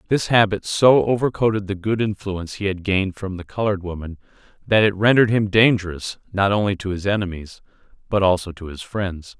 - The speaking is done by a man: Yes, male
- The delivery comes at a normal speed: Yes, average, 190 wpm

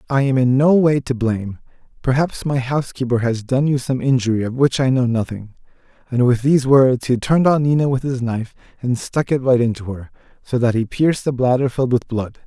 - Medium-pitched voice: No, low, 130 Hz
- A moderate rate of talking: No, fast, 220 wpm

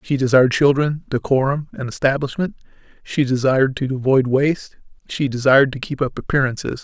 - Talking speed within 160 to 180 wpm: No, average, 150 wpm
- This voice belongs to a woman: No, male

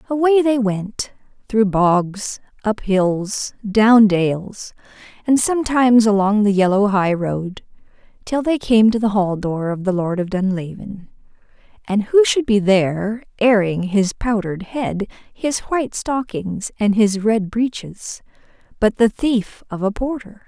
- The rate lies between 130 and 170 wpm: Yes, average, 145 wpm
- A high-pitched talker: Yes, high, 210 Hz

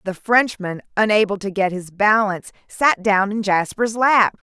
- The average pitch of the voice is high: Yes, high, 205 Hz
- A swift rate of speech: No, average, 160 wpm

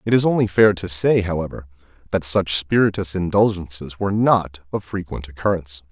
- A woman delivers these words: No, male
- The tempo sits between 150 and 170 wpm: Yes, average, 160 wpm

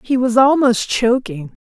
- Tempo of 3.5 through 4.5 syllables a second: Yes, 4.1 syllables/s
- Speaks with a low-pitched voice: No, high, 240 Hz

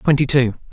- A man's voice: Yes, male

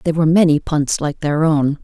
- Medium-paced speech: No, fast, 230 wpm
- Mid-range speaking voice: Yes, medium, 155 Hz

